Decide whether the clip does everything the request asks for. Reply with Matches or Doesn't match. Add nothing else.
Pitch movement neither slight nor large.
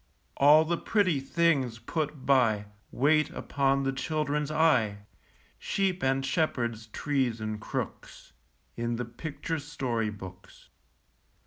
Matches